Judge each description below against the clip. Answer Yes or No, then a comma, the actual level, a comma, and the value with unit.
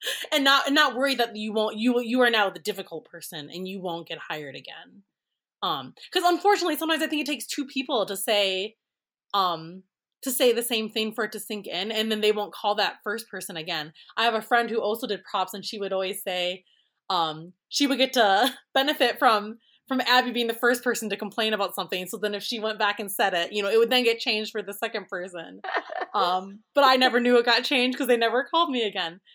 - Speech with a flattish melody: No, average, 4.0 semitones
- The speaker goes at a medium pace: No, fast, 240 wpm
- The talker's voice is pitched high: Yes, high, 220 Hz